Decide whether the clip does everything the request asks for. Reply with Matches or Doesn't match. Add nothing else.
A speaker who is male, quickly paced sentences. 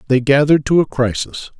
Doesn't match